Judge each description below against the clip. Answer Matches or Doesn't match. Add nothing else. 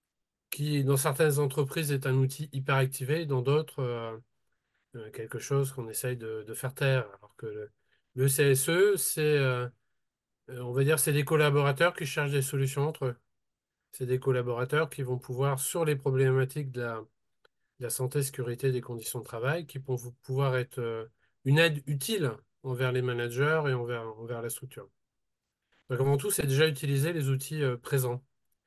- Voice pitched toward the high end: Doesn't match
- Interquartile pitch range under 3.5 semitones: Matches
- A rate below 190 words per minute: Matches